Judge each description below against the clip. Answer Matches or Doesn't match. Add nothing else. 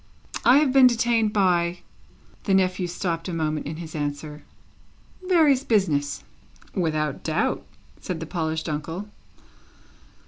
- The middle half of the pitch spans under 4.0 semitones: Doesn't match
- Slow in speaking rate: Matches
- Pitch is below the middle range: Doesn't match